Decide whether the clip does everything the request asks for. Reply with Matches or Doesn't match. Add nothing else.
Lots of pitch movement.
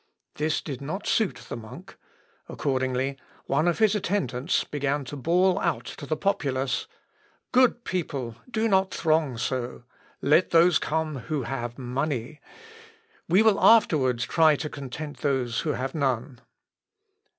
Doesn't match